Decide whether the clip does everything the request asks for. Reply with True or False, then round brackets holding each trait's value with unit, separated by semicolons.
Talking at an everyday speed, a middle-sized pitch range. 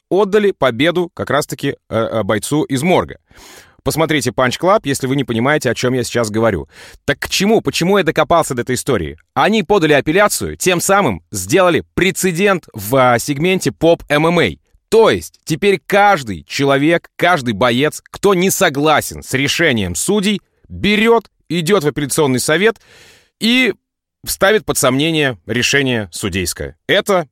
False (135 wpm; 7.0 semitones)